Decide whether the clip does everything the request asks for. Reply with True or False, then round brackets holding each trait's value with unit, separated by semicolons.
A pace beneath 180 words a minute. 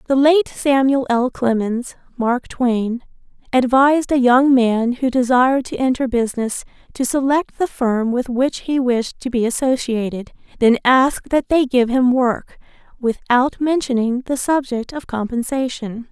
True (150 wpm)